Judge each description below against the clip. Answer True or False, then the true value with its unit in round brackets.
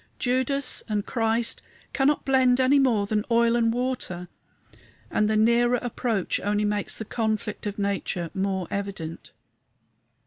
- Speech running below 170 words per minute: True (135 wpm)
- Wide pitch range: False (3.5 semitones)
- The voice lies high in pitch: True (220 Hz)